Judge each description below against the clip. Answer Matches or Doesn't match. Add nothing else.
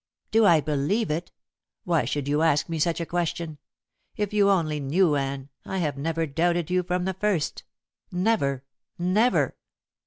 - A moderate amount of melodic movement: Matches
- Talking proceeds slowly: Doesn't match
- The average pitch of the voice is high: Doesn't match